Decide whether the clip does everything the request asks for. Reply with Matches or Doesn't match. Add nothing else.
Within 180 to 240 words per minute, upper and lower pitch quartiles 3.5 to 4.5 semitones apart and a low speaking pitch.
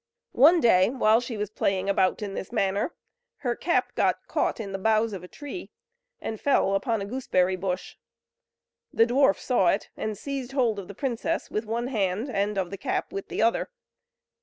Doesn't match